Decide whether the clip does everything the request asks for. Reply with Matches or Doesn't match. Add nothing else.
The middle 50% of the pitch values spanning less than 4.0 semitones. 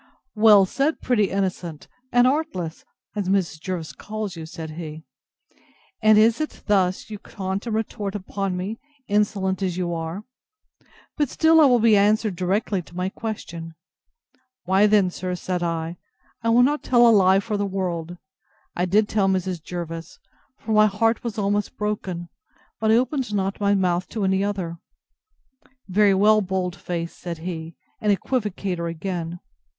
Matches